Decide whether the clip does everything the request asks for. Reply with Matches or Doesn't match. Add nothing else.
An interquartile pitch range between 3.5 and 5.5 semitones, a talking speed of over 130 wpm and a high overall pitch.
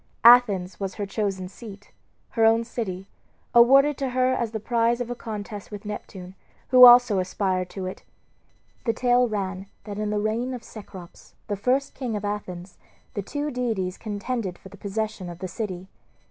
Matches